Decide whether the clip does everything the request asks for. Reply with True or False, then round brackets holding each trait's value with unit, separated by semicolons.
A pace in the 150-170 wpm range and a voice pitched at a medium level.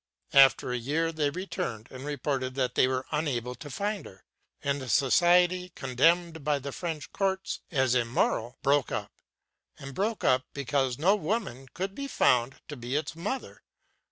True (165 wpm; 145 Hz)